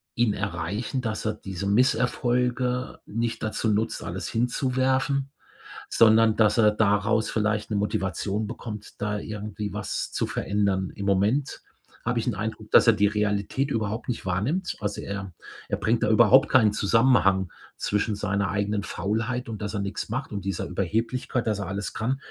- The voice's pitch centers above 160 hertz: No, low, 105 Hz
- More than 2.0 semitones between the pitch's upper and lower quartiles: Yes, average, 2.7 semitones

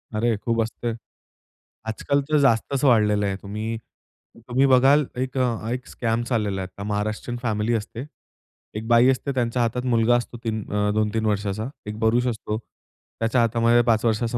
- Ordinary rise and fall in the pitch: No, narrow, 2.2 semitones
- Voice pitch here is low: Yes, low, 115 Hz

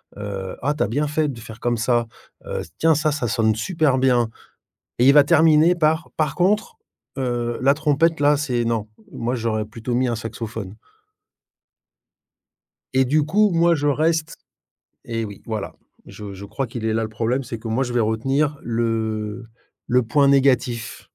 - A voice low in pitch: Yes, low, 125 Hz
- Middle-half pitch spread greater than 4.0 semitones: Yes, average, 4.7 semitones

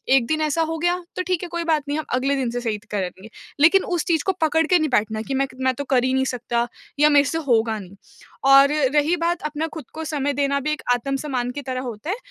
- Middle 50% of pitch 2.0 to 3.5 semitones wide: No, average, 4.1 semitones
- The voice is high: Yes, very high, 280 Hz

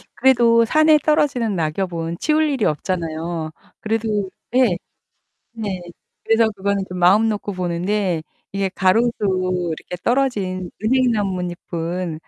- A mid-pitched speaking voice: No, high, 200 Hz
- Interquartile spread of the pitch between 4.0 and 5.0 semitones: Yes, average, 4.6 semitones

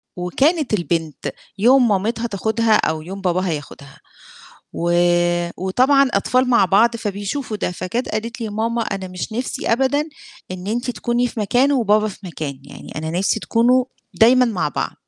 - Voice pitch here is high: Yes, high, 220 Hz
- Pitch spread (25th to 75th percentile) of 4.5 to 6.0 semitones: Yes, average, 4.8 semitones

